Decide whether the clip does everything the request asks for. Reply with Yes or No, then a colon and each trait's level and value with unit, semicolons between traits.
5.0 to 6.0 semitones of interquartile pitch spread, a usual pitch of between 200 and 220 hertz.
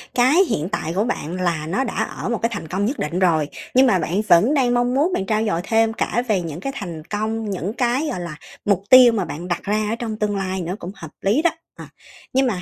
Yes: wide, 5.4 semitones; high, 210 Hz